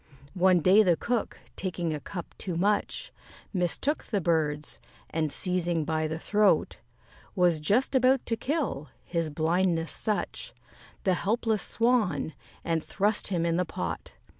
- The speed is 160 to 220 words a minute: No, average, 140 wpm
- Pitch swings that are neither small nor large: Yes, average, 4.4 semitones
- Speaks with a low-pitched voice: No, medium, 180 Hz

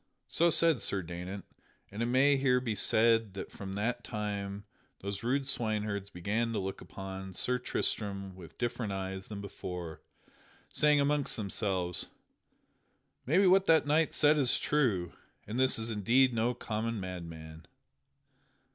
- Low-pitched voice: Yes, low, 110 Hz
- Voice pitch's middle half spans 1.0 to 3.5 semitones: No, average, 4.7 semitones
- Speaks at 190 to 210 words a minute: No, average, 145 wpm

